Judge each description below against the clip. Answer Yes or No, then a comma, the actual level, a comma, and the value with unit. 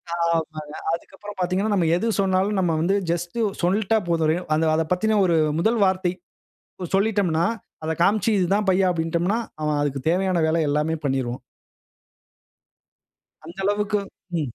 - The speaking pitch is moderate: Yes, medium, 175 Hz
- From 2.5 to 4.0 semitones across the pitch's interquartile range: Yes, average, 3.5 semitones